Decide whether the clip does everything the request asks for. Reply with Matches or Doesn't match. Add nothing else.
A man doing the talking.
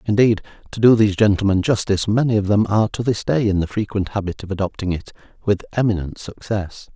Matches